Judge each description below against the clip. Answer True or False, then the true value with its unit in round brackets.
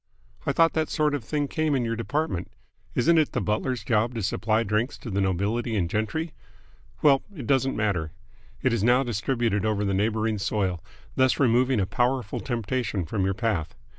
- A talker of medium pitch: False (115 Hz)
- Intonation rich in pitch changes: False (4.3 semitones)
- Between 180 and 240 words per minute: True (185 wpm)